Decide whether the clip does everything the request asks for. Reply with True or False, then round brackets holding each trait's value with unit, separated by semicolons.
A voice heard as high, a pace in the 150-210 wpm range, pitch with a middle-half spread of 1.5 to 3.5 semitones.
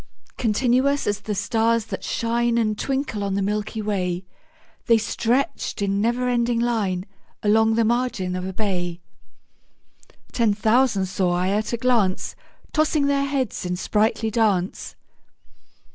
False (220 Hz; 140 wpm; 3.2 semitones)